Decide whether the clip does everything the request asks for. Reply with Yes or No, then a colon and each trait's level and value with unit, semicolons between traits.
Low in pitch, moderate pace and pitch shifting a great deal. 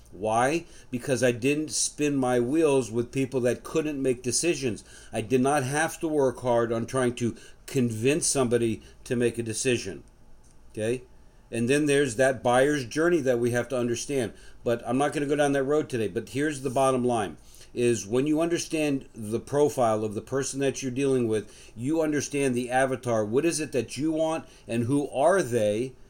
No: low, 130 Hz; average, 190 wpm; average, 3.2 semitones